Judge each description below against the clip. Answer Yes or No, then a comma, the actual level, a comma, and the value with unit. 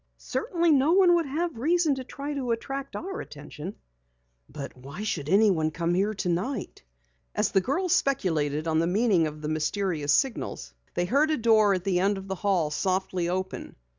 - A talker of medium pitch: No, high, 195 Hz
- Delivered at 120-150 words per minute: No, average, 180 wpm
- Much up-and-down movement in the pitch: Yes, wide, 8.5 semitones